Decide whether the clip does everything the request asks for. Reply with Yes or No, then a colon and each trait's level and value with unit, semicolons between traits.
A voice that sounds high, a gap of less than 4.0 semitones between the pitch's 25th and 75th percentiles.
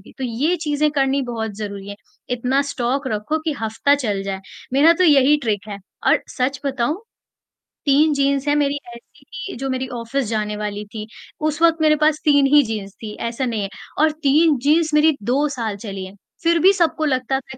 No: very high, 270 Hz; average, 5.1 semitones